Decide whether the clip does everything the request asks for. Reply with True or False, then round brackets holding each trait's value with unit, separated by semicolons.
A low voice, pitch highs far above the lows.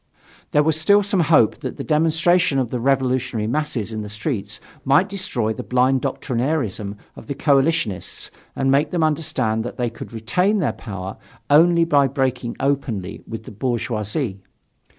True (130 Hz; 5.7 semitones)